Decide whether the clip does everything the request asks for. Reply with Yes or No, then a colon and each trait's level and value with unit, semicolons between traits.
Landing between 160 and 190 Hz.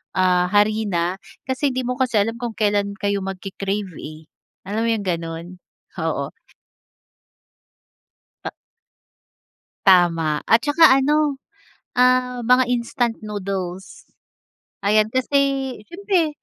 No: high, 215 Hz